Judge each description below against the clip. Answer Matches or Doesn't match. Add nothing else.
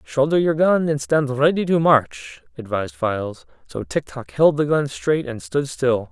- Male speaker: Matches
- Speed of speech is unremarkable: Matches